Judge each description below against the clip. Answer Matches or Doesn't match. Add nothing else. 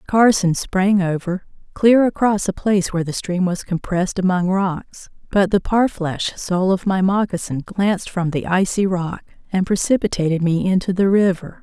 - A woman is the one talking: Matches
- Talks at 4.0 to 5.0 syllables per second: Matches